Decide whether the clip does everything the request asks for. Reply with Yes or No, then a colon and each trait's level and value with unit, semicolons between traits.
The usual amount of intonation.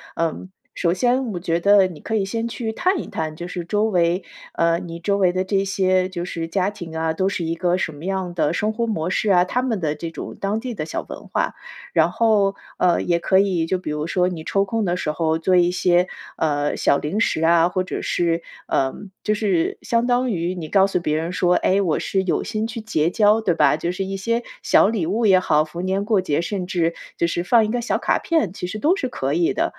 Yes: average, 3.7 semitones